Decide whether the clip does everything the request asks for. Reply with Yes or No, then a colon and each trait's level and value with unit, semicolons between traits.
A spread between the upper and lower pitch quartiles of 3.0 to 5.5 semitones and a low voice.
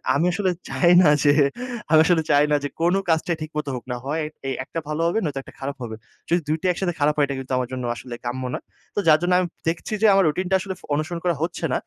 No: average, 3.6 semitones; medium, 155 Hz